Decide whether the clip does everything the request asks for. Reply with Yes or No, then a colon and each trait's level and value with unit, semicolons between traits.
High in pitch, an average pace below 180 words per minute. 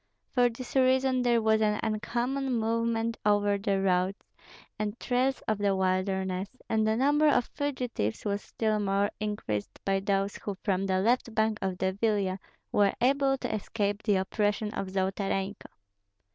Yes: high, 210 Hz; average, 160 wpm